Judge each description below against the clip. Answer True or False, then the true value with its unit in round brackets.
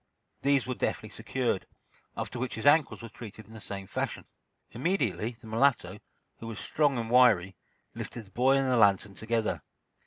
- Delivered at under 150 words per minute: False (175 wpm)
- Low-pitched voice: True (115 Hz)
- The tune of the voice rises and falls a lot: False (3.1 semitones)